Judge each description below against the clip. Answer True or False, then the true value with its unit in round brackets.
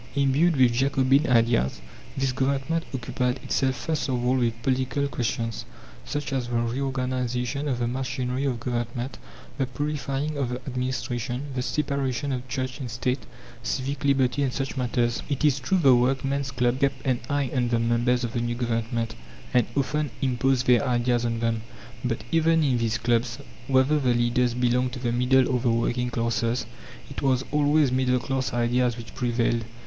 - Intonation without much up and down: True (2.1 semitones)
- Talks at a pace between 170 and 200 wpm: True (175 wpm)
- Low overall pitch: True (125 Hz)